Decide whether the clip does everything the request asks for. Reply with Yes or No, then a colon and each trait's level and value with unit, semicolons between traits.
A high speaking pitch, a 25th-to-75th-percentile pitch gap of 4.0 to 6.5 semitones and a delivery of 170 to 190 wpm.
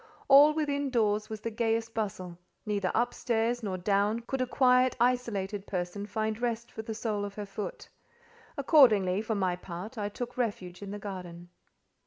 No: high, 215 Hz; average, 3.3 semitones; average, 175 wpm